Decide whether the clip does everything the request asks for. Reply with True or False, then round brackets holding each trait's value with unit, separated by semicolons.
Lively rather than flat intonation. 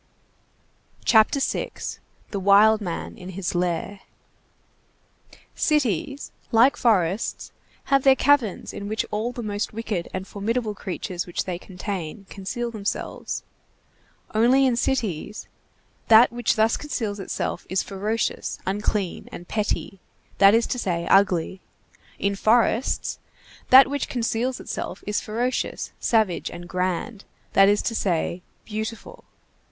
False (3.7 semitones)